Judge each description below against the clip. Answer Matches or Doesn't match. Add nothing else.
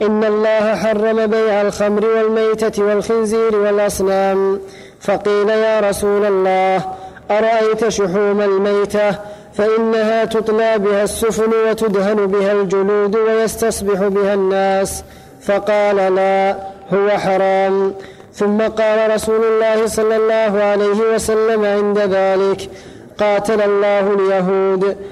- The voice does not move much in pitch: Matches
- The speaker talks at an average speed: Matches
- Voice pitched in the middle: Doesn't match